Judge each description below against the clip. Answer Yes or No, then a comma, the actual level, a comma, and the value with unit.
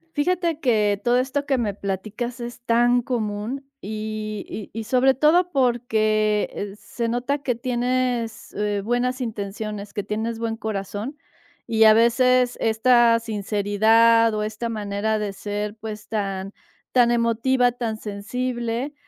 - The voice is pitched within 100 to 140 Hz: No, high, 230 Hz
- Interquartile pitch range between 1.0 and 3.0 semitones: Yes, average, 2.7 semitones